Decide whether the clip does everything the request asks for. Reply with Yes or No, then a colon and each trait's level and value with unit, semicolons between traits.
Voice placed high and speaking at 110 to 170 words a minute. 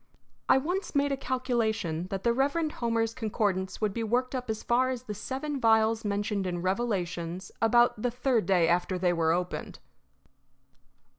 Yes: high, 225 Hz; average, 165 wpm